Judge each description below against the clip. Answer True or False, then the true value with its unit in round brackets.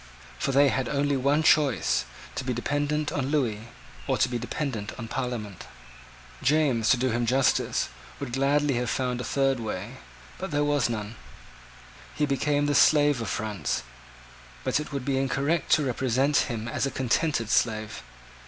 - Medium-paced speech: True (170 wpm)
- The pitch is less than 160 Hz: True (135 Hz)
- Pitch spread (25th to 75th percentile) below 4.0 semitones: True (3.5 semitones)